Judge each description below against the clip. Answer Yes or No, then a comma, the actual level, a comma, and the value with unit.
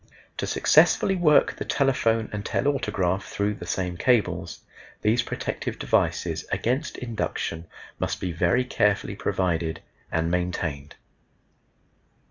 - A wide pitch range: Yes, wide, 6.0 semitones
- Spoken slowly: Yes, slow, 110 wpm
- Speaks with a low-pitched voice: Yes, low, 100 Hz